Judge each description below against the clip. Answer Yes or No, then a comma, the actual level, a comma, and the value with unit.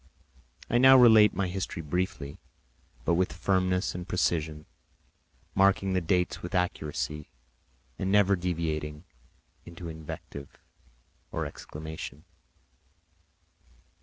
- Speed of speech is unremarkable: No, slow, 100 wpm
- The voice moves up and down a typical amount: Yes, average, 3.7 semitones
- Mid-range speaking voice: No, very low, 90 Hz